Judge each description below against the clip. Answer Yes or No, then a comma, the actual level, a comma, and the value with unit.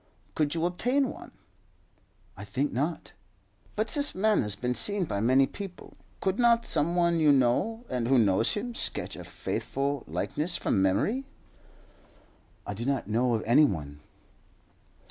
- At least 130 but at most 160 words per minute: Yes, average, 155 wpm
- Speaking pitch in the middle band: Yes, medium, 145 Hz